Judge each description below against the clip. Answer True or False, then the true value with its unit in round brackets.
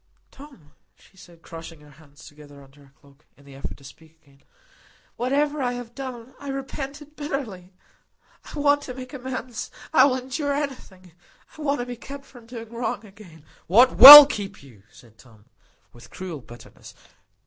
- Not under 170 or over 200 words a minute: True (175 wpm)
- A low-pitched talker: False (230 Hz)